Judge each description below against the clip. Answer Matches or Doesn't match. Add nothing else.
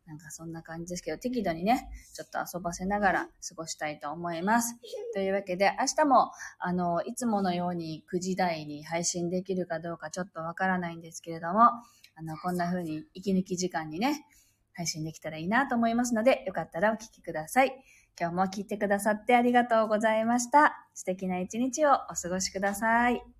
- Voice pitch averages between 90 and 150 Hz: Doesn't match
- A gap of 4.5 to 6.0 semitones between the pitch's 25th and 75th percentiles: Matches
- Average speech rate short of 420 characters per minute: Matches